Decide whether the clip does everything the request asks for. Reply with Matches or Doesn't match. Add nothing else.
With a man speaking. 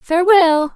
Doesn't match